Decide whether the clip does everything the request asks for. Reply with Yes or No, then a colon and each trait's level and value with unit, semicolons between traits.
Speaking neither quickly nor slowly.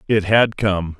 Yes: average, 180 wpm